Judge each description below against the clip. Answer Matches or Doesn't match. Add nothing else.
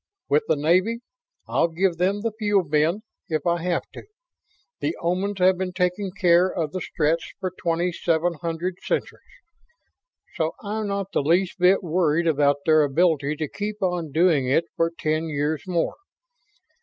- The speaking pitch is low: Doesn't match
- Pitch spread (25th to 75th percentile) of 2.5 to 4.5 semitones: Matches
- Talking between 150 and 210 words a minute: Matches